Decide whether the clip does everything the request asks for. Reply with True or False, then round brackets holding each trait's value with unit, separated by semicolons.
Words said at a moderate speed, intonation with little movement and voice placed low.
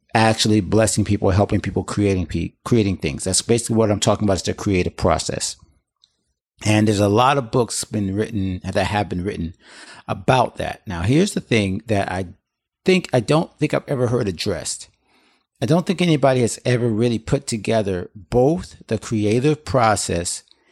False (170 wpm; 4.2 semitones; 110 Hz)